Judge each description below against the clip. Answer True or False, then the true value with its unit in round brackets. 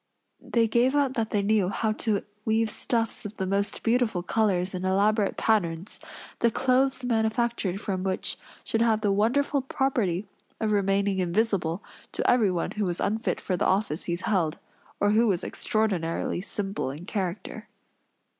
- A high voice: True (210 Hz)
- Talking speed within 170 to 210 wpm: False (155 wpm)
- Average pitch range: True (3.3 semitones)